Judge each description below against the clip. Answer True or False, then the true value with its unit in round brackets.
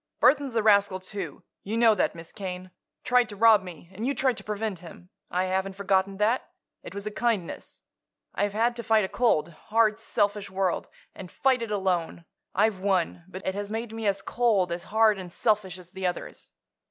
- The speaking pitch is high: True (200 Hz)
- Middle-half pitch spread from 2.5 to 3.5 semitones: True (3.0 semitones)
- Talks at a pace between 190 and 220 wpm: True (200 wpm)